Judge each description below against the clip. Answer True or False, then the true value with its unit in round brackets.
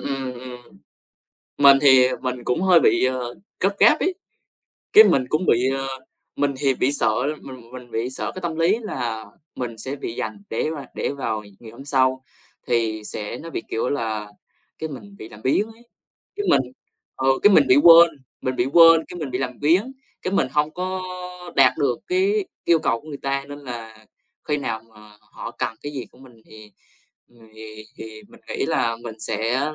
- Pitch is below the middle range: True (130 Hz)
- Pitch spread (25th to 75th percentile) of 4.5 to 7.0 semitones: True (5.0 semitones)